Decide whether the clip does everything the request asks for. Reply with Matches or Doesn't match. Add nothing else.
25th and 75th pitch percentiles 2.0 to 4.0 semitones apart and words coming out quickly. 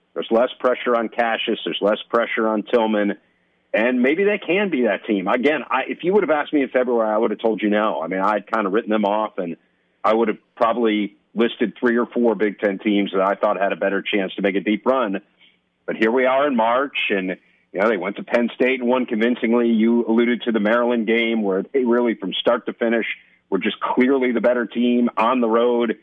Matches